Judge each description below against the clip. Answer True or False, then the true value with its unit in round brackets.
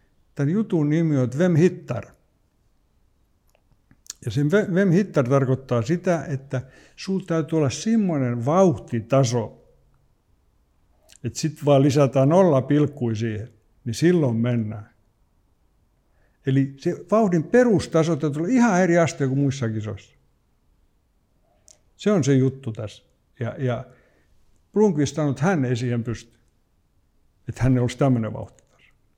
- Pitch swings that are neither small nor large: False (5.8 semitones)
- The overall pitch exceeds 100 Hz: True (135 Hz)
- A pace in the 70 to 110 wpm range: False (120 wpm)